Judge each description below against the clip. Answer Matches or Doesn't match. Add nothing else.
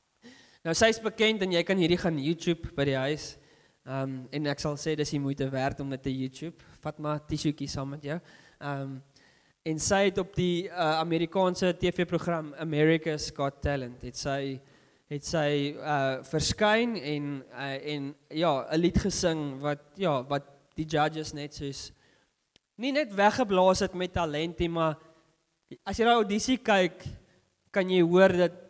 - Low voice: Doesn't match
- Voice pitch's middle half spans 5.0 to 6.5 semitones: Doesn't match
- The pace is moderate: Matches